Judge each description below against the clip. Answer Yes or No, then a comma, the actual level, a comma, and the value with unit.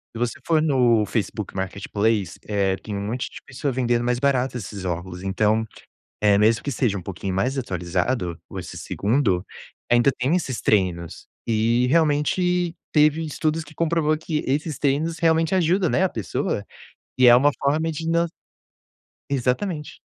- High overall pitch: No, low, 125 Hz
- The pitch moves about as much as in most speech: No, wide, 6.8 semitones